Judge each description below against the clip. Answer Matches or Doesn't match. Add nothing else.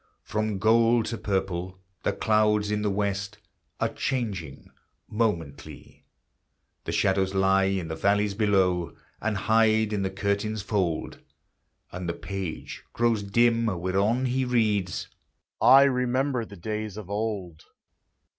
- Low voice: Matches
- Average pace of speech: Doesn't match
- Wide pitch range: Doesn't match